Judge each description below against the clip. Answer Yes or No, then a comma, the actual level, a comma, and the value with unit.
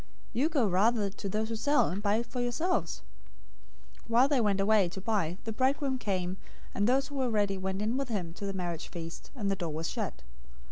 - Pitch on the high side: Yes, high, 210 Hz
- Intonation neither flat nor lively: Yes, average, 4.3 semitones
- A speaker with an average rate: No, fast, 220 wpm